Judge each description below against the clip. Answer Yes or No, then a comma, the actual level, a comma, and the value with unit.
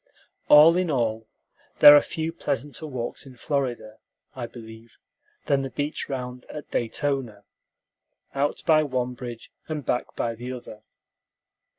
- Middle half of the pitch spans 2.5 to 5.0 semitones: Yes, average, 3.7 semitones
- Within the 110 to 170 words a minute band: Yes, slow, 135 wpm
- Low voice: Yes, low, 130 Hz